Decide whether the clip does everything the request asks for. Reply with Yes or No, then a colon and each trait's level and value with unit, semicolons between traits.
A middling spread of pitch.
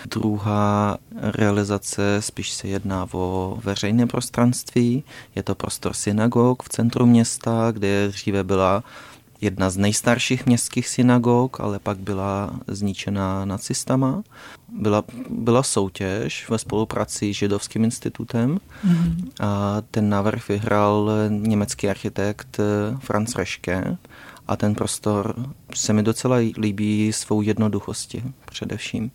Yes: average, 3.0 semitones